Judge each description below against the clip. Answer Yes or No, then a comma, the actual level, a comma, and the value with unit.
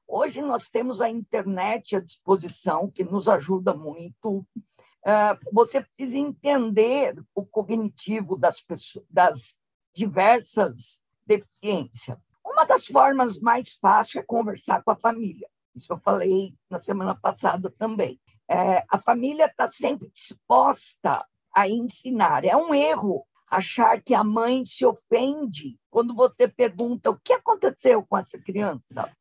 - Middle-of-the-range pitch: No, high, 220 Hz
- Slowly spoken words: No, average, 130 wpm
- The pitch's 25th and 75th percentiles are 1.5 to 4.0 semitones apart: No, average, 4.7 semitones